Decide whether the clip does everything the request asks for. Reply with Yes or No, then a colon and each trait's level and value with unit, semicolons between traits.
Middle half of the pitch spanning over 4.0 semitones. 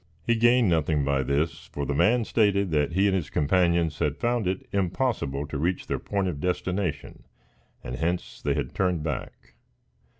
Yes: average, 5.1 semitones